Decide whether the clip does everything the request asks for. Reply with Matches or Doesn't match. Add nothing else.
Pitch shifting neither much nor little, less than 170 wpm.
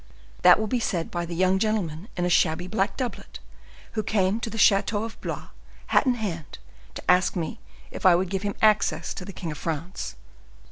Doesn't match